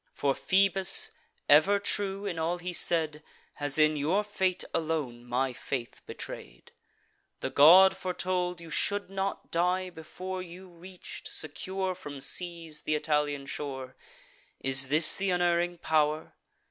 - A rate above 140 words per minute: No, slow, 135 wpm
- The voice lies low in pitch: No, medium, 170 Hz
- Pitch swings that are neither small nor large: Yes, average, 3.8 semitones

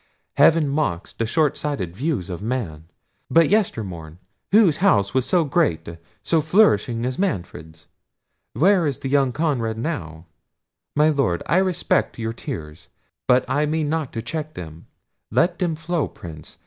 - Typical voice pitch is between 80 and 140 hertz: Yes, low, 135 Hz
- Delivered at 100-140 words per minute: Yes, slow, 135 wpm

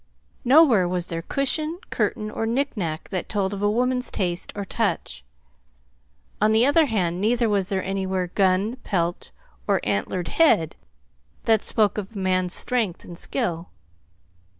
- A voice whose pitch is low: No, high, 200 Hz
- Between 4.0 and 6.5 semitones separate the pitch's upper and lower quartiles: Yes, average, 4.5 semitones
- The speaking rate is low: No, average, 150 wpm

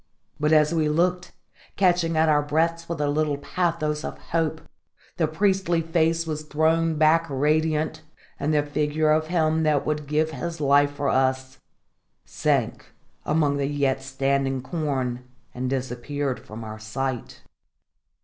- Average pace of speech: Yes, average, 145 wpm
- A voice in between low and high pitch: Yes, medium, 150 Hz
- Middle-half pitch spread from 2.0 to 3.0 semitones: Yes, narrow, 2.6 semitones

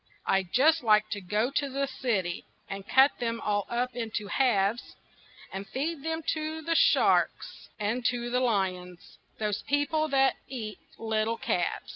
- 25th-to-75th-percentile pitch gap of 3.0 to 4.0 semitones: No, average, 4.8 semitones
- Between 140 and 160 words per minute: Yes, average, 145 wpm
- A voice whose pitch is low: No, high, 230 Hz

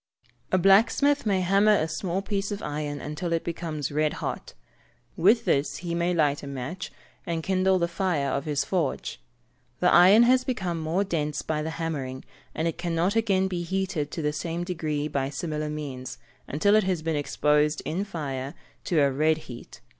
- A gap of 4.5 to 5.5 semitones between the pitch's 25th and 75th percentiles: No, average, 4.1 semitones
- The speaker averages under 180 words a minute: No, average, 185 wpm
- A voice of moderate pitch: Yes, medium, 165 Hz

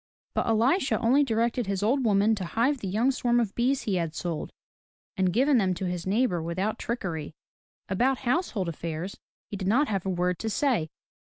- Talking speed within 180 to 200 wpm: Yes, average, 190 wpm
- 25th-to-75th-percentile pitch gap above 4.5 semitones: Yes, average, 5.1 semitones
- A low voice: No, high, 210 Hz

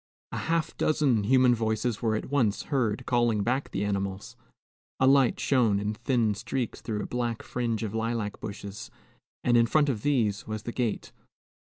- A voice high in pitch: No, low, 115 Hz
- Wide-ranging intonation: No, average, 3.3 semitones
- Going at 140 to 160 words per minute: No, average, 175 wpm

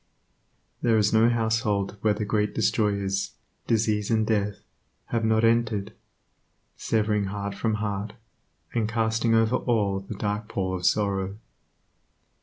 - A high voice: No, low, 105 Hz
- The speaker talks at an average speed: No, slow, 130 wpm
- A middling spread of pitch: No, narrow, 1.8 semitones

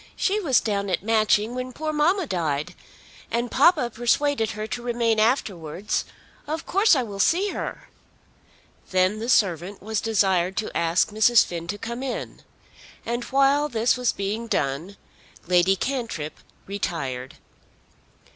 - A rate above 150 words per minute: No, average, 145 wpm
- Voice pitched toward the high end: Yes, high, 220 Hz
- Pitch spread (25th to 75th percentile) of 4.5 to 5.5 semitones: Yes, average, 5.2 semitones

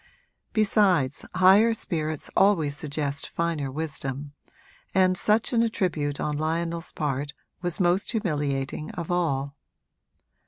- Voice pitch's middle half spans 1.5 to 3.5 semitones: No, average, 4.3 semitones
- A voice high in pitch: No, medium, 160 Hz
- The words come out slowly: Yes, slow, 110 wpm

